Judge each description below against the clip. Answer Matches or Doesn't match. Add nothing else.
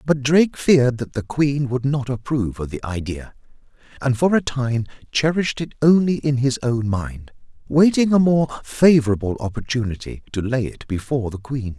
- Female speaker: Doesn't match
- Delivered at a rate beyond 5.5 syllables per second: Doesn't match